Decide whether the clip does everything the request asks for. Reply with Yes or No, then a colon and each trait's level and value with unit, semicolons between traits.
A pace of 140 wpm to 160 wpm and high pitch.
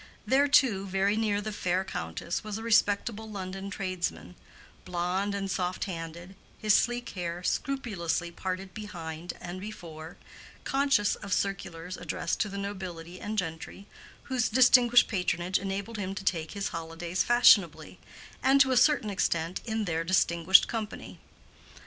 Yes: average, 145 wpm; high, 195 Hz